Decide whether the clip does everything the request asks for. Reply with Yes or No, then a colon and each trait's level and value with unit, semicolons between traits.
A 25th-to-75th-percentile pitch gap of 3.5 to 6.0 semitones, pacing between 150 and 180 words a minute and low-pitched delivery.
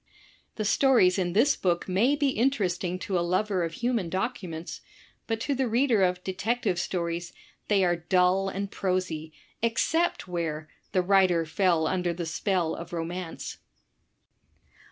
No: average, 3.8 semitones; average, 155 wpm; medium, 185 Hz